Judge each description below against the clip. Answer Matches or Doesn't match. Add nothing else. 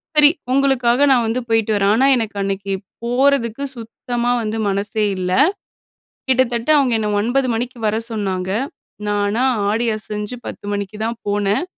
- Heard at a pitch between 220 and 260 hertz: Matches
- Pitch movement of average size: Matches